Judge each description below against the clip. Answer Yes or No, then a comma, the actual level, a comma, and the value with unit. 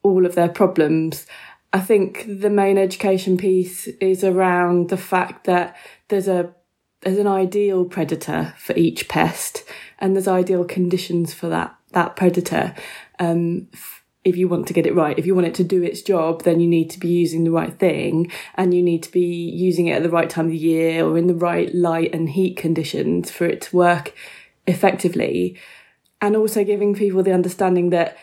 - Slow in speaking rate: No, average, 195 wpm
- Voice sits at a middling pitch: Yes, medium, 180 Hz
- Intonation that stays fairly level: Yes, narrow, 2.0 semitones